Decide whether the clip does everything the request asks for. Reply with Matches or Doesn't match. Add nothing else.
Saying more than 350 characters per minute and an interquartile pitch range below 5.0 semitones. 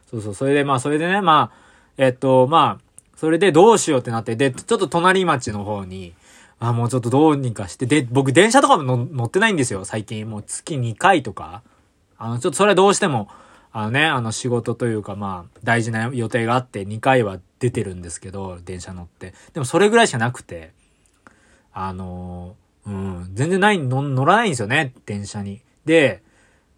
Doesn't match